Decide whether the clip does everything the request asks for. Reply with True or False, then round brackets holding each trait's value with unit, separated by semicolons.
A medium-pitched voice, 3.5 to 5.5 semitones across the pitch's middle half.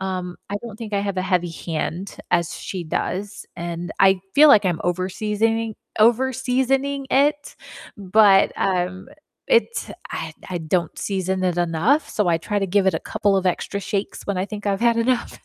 False (195 Hz; 4.0 semitones)